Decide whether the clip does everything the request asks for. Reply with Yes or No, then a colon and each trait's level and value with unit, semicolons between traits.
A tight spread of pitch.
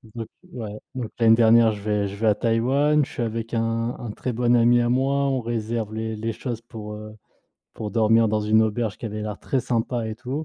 Yes: narrow, 1.9 semitones